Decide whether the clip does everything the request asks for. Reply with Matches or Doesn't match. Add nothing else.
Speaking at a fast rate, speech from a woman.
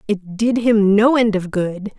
Matches